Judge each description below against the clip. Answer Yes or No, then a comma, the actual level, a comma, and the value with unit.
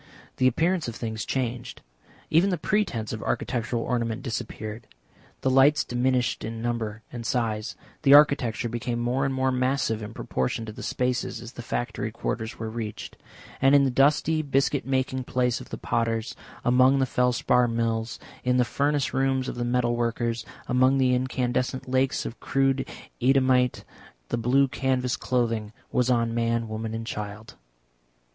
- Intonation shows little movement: Yes, narrow, 2.3 semitones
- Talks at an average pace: Yes, average, 160 wpm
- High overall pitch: No, low, 125 Hz